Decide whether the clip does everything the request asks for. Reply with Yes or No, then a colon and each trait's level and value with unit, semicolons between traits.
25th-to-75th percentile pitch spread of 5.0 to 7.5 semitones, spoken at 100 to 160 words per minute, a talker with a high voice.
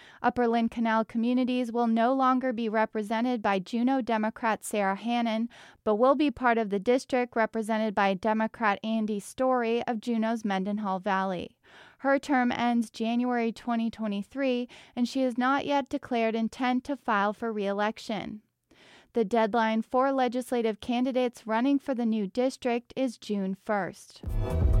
No: narrow, 2.4 semitones; average, 145 wpm; high, 230 Hz